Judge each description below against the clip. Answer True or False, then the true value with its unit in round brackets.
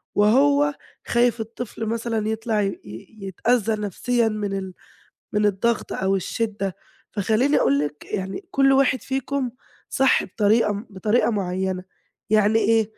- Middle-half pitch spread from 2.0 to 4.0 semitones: True (3.5 semitones)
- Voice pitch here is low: False (215 Hz)